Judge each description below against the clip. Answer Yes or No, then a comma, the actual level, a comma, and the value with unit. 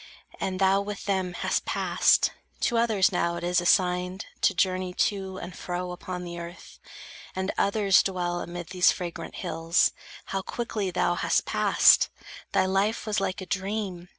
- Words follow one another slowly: No, average, 160 wpm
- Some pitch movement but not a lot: No, narrow, 1.7 semitones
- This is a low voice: No, medium, 185 Hz